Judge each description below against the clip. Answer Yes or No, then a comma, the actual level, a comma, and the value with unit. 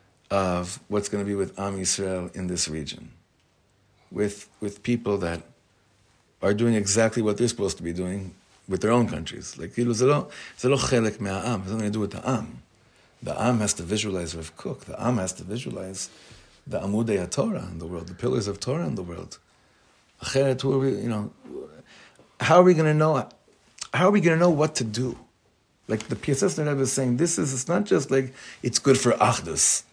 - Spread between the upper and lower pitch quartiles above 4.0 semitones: Yes, average, 5.3 semitones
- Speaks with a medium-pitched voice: No, low, 110 Hz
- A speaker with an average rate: Yes, average, 185 wpm